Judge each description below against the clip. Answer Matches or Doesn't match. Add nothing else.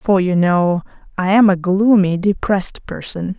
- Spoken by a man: Doesn't match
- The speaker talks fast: Doesn't match